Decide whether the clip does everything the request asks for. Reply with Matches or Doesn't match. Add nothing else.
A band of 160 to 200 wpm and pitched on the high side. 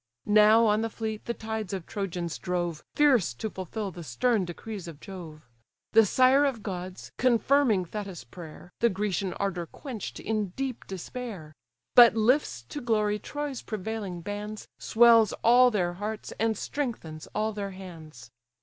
Doesn't match